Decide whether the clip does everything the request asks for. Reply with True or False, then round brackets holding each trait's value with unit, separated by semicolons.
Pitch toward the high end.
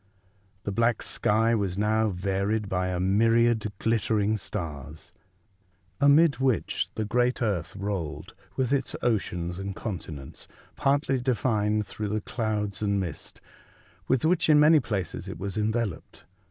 False (105 Hz)